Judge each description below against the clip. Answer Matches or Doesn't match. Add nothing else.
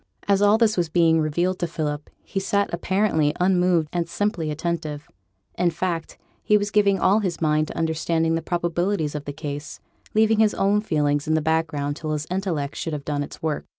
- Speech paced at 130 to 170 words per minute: Doesn't match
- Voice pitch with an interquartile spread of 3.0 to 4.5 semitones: Matches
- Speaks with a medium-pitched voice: Matches